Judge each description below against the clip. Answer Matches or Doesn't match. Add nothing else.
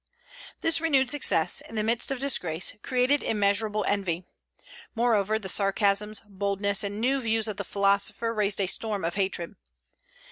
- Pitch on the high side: Matches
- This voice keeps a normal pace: Matches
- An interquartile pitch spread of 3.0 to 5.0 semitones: Doesn't match